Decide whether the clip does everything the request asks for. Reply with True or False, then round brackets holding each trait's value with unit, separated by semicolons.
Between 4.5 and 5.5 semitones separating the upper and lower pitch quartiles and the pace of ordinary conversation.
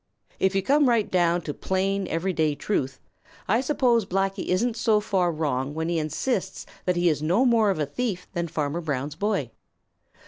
True (5.1 semitones; 180 wpm)